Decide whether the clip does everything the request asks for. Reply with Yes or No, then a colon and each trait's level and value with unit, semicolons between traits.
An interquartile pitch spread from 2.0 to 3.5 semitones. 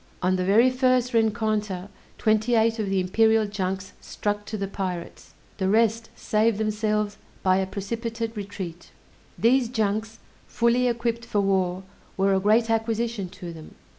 Yes: average, 2.9 semitones